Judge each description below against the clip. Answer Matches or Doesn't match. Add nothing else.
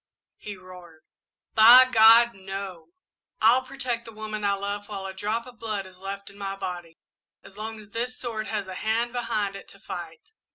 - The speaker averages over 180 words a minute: Matches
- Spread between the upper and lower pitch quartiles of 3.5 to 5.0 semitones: Doesn't match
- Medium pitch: Doesn't match